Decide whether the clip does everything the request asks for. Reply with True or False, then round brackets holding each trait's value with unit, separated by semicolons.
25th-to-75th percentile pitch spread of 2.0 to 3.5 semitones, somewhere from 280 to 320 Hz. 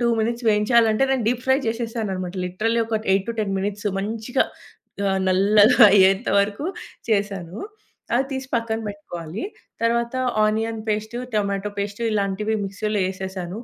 False (2.8 semitones; 215 Hz)